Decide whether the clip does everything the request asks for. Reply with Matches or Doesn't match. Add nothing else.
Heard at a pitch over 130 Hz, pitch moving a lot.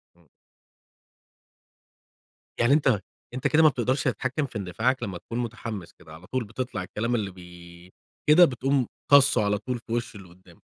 Doesn't match